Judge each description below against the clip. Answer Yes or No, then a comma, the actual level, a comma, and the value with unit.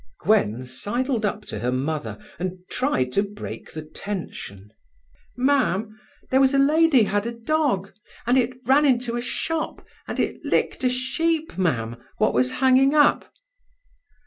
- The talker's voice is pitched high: Yes, high, 230 Hz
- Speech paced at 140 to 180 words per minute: Yes, average, 150 wpm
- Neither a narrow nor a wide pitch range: No, wide, 8.8 semitones